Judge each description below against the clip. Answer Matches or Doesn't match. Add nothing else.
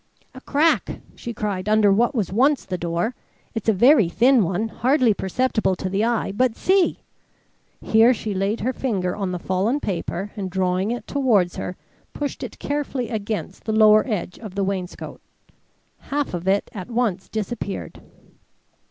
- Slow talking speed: Doesn't match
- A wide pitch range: Doesn't match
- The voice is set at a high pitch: Matches